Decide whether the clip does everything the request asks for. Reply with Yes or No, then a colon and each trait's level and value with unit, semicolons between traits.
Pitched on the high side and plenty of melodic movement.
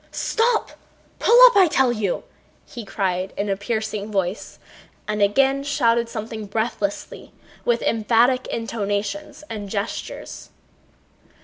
No: high, 220 Hz; average, 3.8 semitones